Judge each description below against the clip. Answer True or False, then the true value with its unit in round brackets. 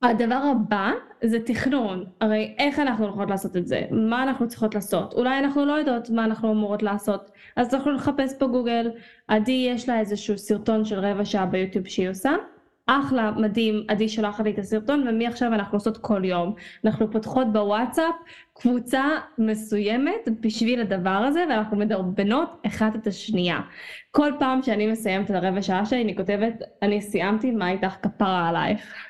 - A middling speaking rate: False (165 wpm)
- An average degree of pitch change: True (3.7 semitones)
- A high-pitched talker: True (220 Hz)